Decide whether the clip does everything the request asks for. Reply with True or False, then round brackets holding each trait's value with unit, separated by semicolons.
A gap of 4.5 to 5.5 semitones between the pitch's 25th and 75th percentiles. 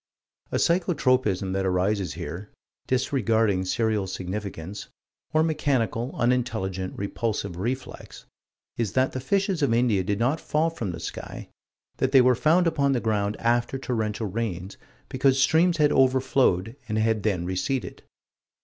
True (4.9 semitones)